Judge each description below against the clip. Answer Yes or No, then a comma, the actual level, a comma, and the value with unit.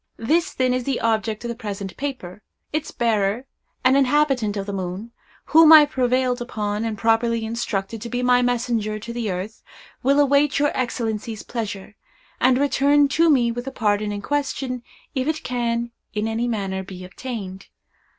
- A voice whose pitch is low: No, high, 235 Hz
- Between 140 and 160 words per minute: No, average, 175 wpm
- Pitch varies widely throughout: No, average, 3.7 semitones